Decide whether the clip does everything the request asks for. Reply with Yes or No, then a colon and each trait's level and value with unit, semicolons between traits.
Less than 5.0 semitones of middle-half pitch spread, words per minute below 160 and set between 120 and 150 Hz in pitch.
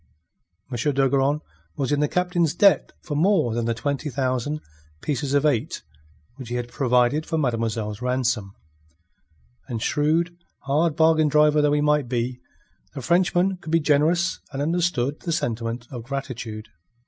Yes: average, 4.4 semitones; average, 150 wpm; medium, 140 Hz